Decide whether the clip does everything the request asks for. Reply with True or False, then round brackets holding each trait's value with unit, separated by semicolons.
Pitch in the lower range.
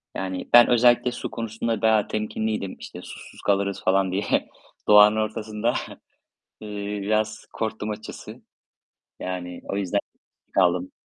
True (105 Hz)